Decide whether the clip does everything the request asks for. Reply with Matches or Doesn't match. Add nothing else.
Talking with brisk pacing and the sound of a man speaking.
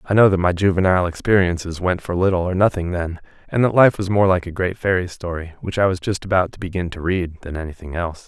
Matches